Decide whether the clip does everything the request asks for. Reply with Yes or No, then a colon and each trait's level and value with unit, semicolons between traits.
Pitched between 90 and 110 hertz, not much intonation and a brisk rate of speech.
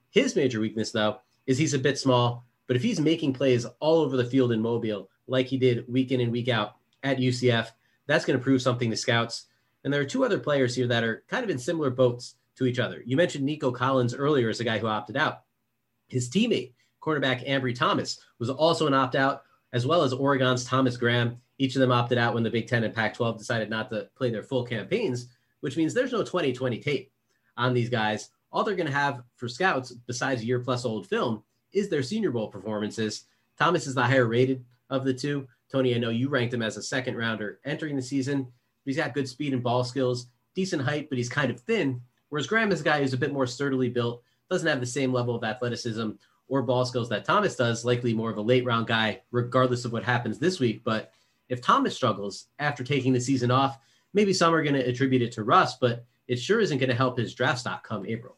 No: low, 125 Hz; narrow, 2.3 semitones; fast, 235 wpm